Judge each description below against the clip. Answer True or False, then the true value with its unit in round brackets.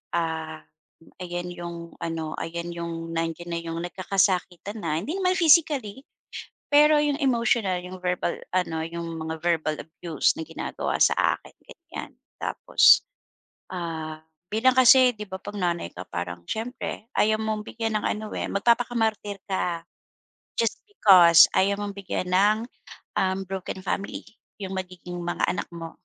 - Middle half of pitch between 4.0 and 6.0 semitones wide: True (4.4 semitones)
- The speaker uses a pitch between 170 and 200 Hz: True (185 Hz)